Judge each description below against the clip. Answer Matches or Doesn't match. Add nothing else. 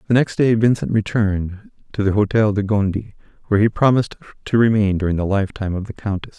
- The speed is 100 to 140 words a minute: Doesn't match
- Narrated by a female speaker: Doesn't match